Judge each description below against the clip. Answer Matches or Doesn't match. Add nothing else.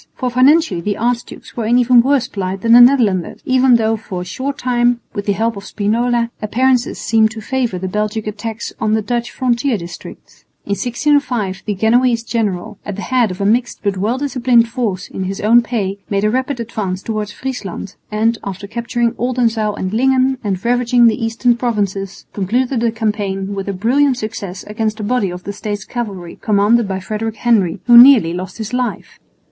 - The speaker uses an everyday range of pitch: Matches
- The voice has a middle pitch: Doesn't match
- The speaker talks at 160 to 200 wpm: Matches